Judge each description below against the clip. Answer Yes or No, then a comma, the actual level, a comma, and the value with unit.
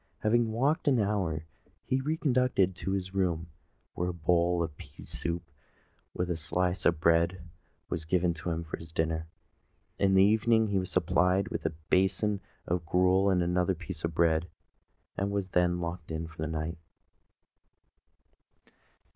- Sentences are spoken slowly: No, average, 165 wpm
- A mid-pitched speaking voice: No, very low, 90 Hz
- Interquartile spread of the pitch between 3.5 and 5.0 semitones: No, average, 2.8 semitones